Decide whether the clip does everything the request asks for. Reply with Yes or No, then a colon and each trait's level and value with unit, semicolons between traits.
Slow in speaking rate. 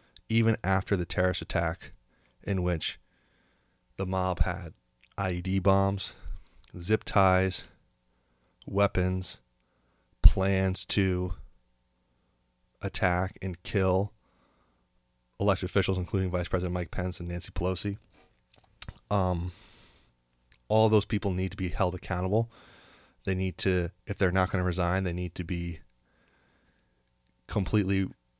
Yes: slow, 110 wpm